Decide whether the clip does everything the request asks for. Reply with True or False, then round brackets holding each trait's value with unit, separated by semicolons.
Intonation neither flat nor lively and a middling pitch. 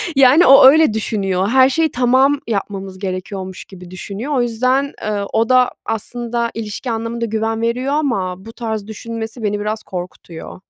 False (4.0 semitones; 225 Hz)